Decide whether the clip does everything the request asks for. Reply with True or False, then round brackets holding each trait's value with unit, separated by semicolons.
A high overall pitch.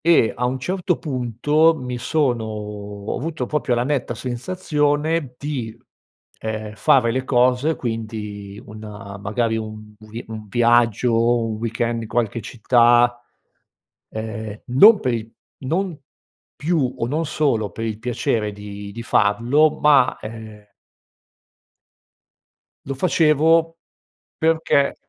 False (120 Hz)